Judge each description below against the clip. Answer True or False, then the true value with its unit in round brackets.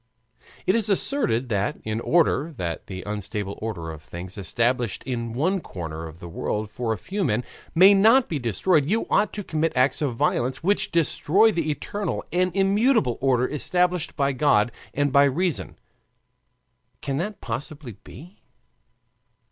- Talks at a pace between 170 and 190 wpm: False (155 wpm)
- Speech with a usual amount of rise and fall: False (8.3 semitones)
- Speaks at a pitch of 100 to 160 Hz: True (140 Hz)